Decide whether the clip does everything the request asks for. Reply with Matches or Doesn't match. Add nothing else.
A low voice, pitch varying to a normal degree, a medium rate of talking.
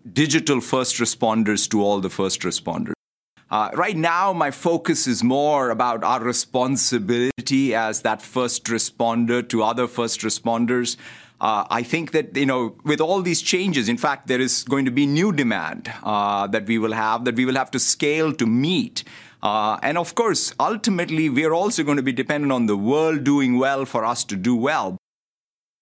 Matches